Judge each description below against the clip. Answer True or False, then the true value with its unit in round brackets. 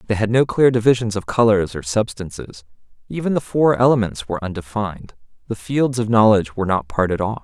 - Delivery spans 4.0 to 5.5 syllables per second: False (6.0 syllables/s)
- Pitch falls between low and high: False (105 Hz)